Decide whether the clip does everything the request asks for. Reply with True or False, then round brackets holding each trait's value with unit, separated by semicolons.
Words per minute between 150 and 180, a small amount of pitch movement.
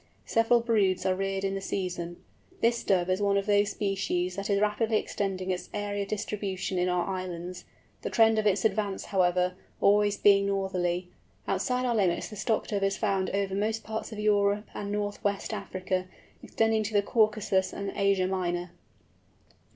True (175 wpm; 2.1 semitones)